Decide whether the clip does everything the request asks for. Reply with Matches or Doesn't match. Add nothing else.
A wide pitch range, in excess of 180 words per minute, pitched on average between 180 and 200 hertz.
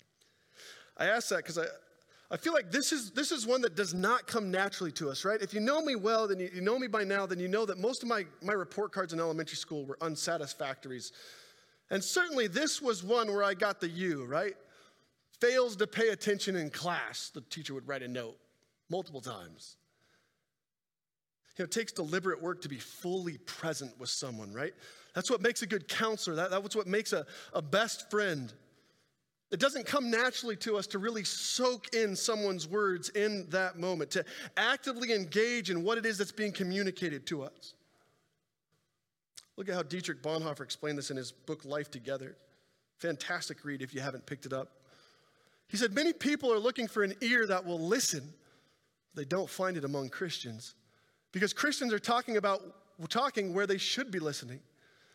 Matches